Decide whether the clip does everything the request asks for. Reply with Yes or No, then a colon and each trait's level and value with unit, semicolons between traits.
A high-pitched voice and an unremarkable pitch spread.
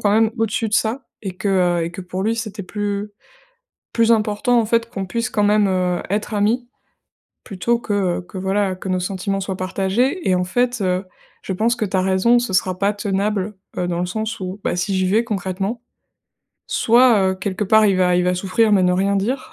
Yes: high, 200 Hz; average, 3.1 semitones